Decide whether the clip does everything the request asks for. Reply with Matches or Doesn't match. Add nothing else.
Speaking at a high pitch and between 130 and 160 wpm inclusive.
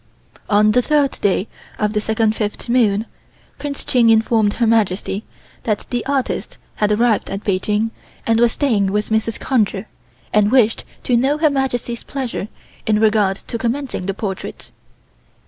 Matches